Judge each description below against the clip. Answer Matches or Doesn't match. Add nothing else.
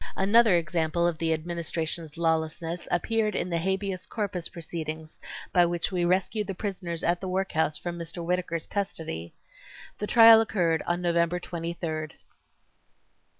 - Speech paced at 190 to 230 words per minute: Doesn't match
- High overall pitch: Doesn't match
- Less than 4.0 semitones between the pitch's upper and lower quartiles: Matches